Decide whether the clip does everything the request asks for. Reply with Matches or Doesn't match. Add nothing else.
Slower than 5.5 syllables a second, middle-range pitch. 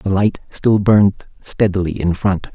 Doesn't match